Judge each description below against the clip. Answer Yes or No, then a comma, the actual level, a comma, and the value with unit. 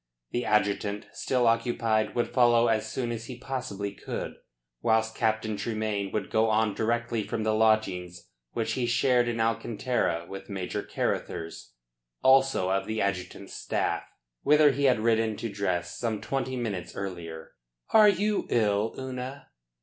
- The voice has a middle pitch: No, low, 110 Hz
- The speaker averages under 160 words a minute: Yes, average, 150 wpm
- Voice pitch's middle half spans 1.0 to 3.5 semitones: Yes, average, 3.1 semitones